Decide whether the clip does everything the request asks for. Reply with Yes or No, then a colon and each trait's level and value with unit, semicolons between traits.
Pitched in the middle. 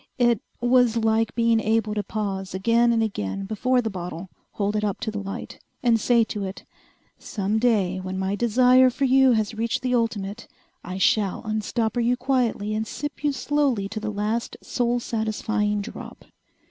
No: high, 220 Hz